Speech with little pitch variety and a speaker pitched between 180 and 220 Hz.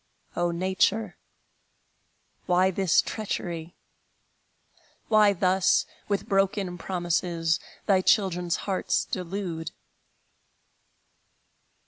Yes: narrow, 2.1 semitones; medium, 185 Hz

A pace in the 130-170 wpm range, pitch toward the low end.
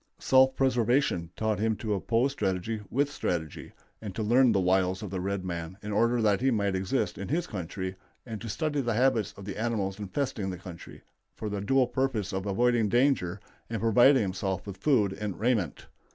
No: average, 190 wpm; low, 105 Hz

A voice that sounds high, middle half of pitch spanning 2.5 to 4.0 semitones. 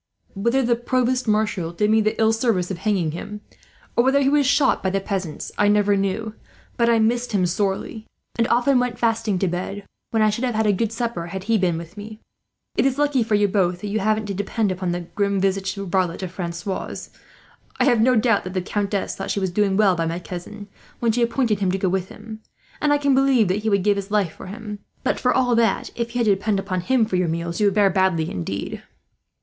Yes: high, 205 Hz; average, 3.5 semitones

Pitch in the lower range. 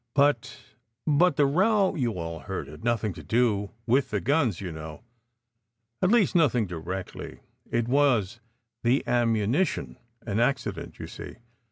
Yes: low, 120 Hz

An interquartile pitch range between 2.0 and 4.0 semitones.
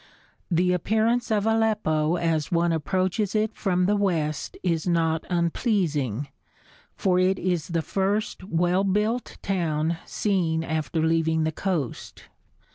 Yes: average, 3.5 semitones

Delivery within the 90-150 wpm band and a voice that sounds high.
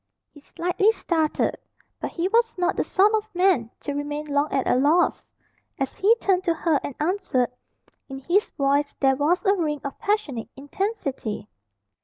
No: average, 170 wpm; very high, 315 Hz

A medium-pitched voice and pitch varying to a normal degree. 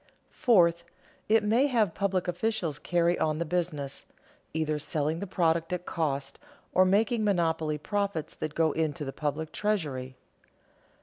Yes: medium, 170 Hz; average, 4.5 semitones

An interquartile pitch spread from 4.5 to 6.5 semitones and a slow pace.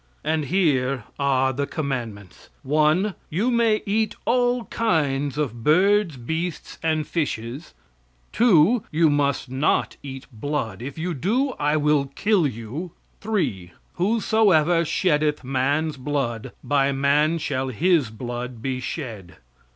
Yes: average, 5.1 semitones; slow, 125 wpm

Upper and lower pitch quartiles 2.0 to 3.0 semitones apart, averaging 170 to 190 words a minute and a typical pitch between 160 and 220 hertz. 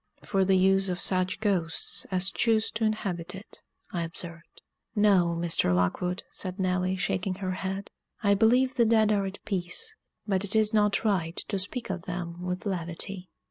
Yes: narrow, 2.5 semitones; average, 175 wpm; high, 190 Hz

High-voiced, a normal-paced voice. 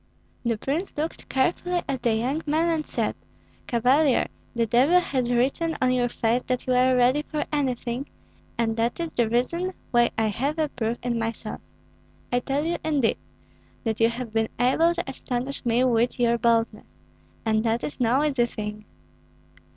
Yes: very high, 250 Hz; average, 175 wpm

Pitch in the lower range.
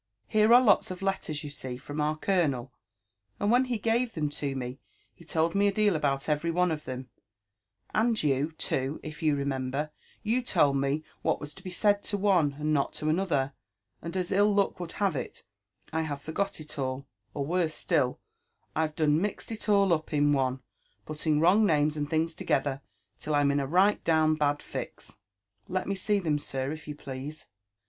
No: medium, 155 Hz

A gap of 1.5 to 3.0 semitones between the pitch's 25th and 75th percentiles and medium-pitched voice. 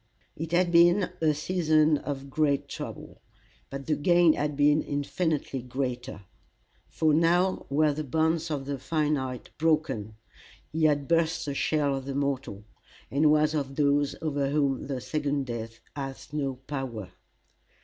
Yes: narrow, 2.4 semitones; medium, 145 Hz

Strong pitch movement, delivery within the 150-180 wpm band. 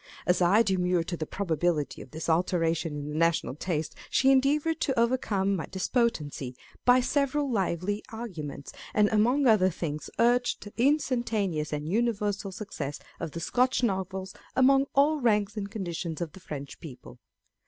Yes: wide, 6.4 semitones; average, 160 wpm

